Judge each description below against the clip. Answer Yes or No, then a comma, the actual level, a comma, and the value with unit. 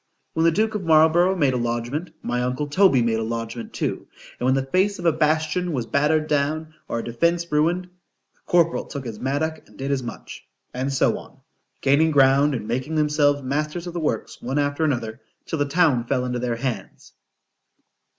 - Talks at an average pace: Yes, average, 180 wpm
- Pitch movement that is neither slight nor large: Yes, average, 4.2 semitones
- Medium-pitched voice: Yes, medium, 145 Hz